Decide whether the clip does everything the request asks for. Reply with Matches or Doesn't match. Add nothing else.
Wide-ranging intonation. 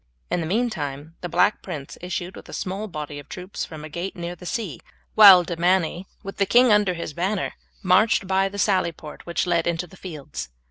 Doesn't match